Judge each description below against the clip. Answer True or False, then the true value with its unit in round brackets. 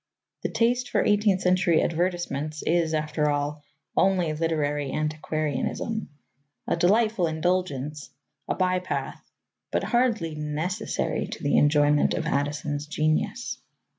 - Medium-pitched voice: True (160 Hz)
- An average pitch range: True (3.6 semitones)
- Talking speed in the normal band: False (115 wpm)